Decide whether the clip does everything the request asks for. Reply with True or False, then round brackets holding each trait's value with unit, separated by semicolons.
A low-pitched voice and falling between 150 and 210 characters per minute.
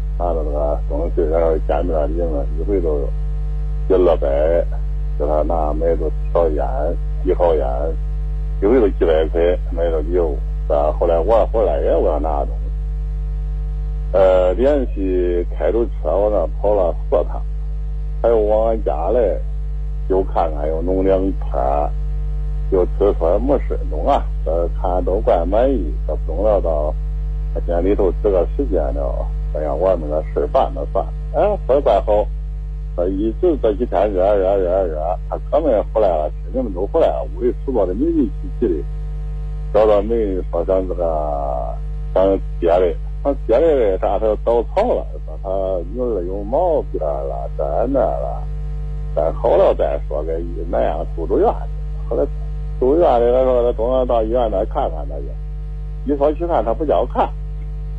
False (95 Hz; 225 characters per minute)